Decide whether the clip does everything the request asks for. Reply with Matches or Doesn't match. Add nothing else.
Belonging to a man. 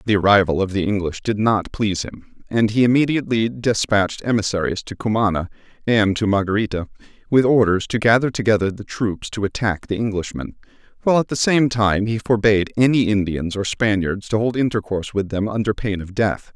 Matches